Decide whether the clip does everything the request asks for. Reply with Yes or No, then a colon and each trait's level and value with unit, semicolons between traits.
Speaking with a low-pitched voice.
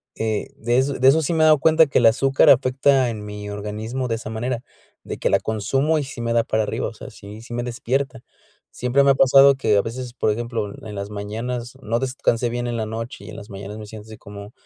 Yes: low, 120 Hz